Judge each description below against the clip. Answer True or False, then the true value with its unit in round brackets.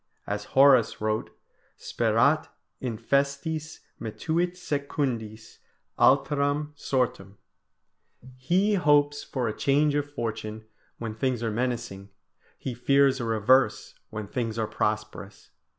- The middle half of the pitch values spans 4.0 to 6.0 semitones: True (4.7 semitones)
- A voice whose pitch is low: True (130 Hz)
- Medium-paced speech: False (105 wpm)